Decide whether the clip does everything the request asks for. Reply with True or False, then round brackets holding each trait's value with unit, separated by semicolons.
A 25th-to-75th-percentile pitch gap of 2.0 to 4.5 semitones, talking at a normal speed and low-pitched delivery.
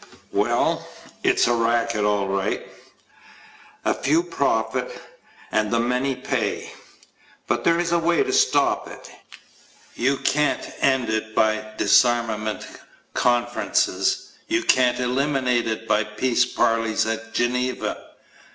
False (3.5 semitones; 120 wpm; 120 Hz)